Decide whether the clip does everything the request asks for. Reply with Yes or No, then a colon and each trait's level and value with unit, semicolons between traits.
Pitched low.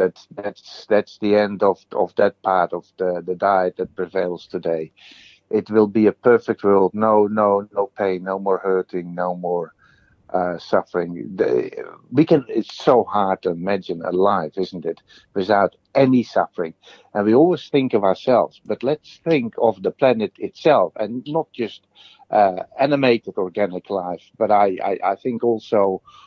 Yes: low, 105 Hz